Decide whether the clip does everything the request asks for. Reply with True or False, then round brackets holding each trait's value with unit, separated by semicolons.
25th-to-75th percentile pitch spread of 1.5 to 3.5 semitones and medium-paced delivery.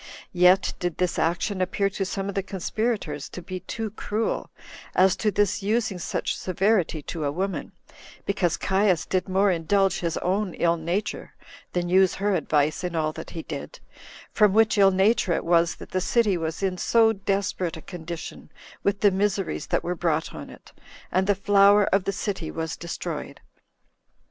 True (2.8 semitones; 180 wpm)